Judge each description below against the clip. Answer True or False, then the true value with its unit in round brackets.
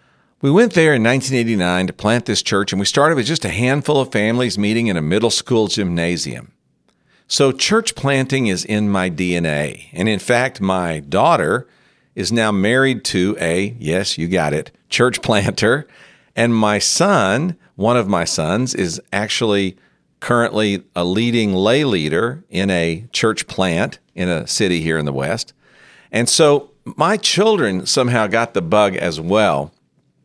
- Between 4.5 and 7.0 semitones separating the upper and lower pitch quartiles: True (5.4 semitones)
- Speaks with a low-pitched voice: True (105 Hz)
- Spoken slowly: False (165 wpm)